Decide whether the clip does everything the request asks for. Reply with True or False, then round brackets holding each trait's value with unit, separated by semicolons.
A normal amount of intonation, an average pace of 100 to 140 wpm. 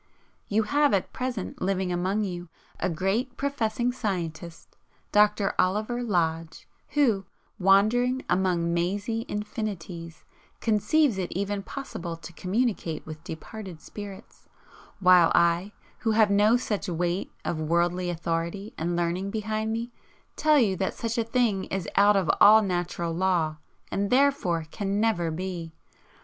True (4.0 semitones; 135 wpm)